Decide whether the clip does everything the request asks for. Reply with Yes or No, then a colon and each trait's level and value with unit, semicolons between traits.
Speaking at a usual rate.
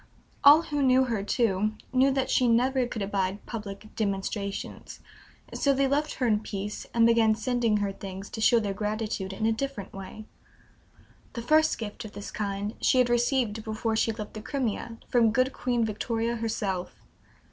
Yes: average, 175 wpm